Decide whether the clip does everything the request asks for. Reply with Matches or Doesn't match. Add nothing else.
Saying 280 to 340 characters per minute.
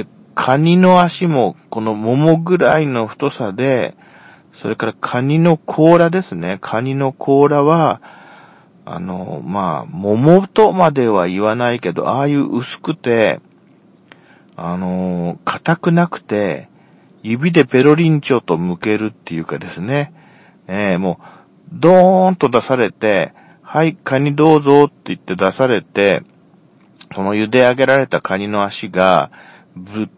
Doesn't match